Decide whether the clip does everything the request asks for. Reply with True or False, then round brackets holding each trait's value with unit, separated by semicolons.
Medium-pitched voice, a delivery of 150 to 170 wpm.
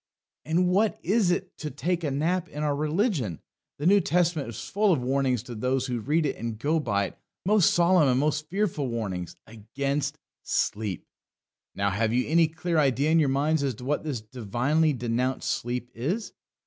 False (145 Hz; 185 wpm)